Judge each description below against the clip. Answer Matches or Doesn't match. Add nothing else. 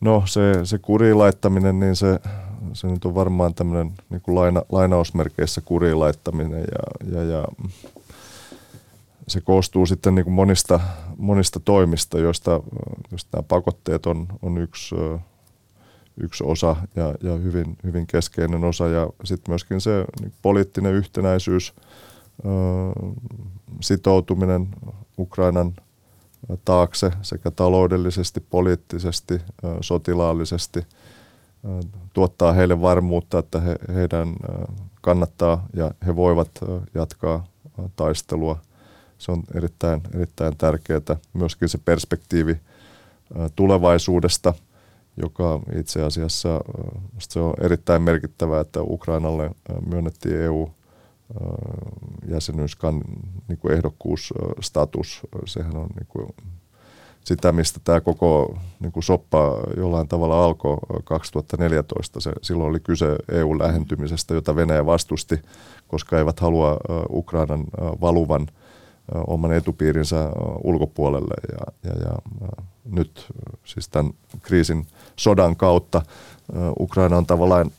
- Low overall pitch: Matches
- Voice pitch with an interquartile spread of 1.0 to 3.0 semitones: Matches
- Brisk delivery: Doesn't match